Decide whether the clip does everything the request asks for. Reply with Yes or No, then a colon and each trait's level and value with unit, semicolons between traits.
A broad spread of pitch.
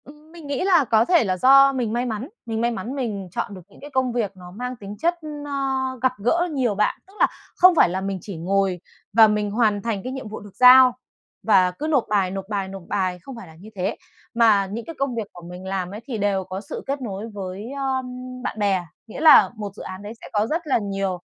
No: average, 5.0 semitones